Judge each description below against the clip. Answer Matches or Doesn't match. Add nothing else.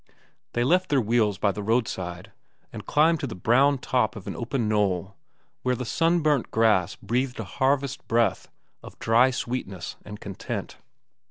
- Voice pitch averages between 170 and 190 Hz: Doesn't match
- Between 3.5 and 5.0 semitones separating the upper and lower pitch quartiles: Matches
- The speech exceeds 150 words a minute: Matches